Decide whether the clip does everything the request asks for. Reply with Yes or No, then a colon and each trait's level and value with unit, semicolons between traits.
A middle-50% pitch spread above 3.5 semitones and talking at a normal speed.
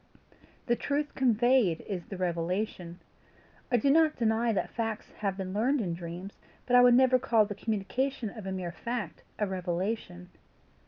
Yes: average, 4.9 semitones; average, 165 wpm